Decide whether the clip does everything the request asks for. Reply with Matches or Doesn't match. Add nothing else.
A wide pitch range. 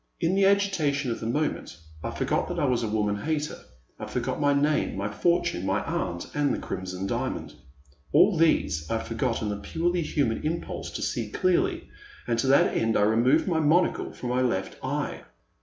Matches